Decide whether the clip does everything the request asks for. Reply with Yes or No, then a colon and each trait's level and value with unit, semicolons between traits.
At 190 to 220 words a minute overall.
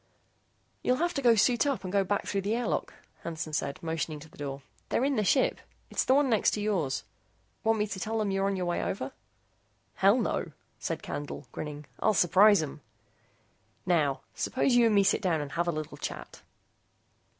Yes: average, 200 wpm